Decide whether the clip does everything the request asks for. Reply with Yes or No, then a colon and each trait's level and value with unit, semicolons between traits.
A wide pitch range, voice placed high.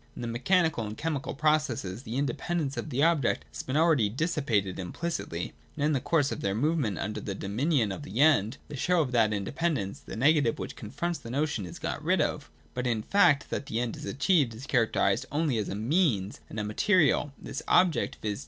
No: wide, 6.3 semitones; low, 130 Hz